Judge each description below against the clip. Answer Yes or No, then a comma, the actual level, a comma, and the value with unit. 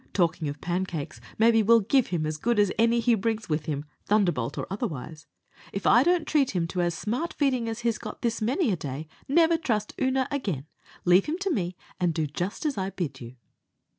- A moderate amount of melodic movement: No, wide, 6.2 semitones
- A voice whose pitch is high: Yes, high, 205 Hz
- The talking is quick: Yes, fast, 210 wpm